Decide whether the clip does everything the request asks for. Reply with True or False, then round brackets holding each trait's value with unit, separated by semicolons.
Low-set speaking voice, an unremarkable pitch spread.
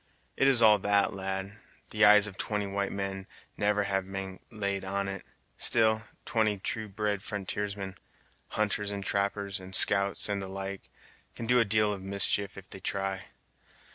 False (100 Hz; 1.3 semitones)